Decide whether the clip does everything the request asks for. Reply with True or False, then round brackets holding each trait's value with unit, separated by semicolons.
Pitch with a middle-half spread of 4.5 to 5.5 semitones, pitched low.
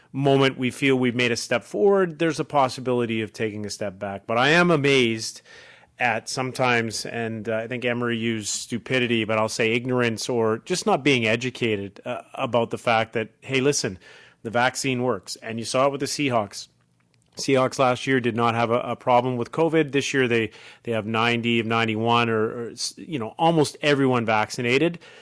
False (2.9 semitones; 120 Hz)